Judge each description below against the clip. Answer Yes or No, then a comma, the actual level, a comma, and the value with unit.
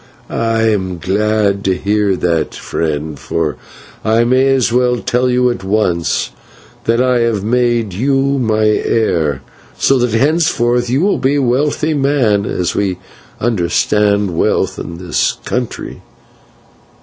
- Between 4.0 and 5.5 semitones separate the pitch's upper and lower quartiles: Yes, average, 4.5 semitones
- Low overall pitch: Yes, low, 110 Hz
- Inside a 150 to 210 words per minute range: No, slow, 135 wpm